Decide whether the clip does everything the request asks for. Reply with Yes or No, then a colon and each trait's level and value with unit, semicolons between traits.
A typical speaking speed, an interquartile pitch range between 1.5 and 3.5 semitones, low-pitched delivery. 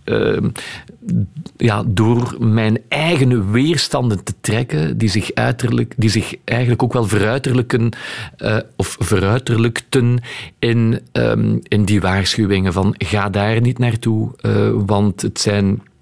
No: slow, 125 wpm; average, 2.9 semitones; low, 115 Hz